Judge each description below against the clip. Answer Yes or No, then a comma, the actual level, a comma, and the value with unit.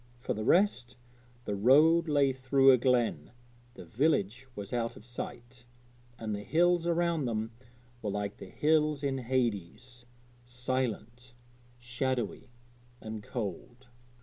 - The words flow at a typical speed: No, slow, 125 wpm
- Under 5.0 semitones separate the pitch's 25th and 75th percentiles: Yes, average, 3.2 semitones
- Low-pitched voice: Yes, low, 125 Hz